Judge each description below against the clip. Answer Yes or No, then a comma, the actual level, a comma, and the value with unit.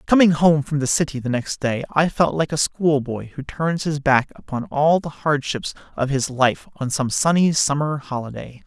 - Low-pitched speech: No, medium, 145 Hz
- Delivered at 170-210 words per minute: Yes, average, 200 wpm